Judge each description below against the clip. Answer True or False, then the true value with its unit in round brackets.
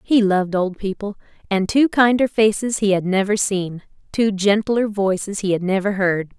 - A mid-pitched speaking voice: False (200 Hz)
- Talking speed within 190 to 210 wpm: False (170 wpm)